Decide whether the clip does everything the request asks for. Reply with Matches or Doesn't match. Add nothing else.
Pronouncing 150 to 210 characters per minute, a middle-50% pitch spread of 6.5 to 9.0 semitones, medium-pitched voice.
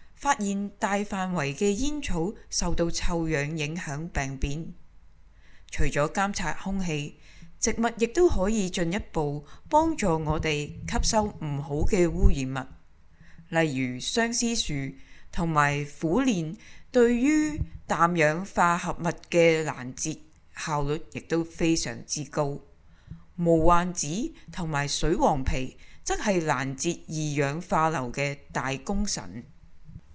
Doesn't match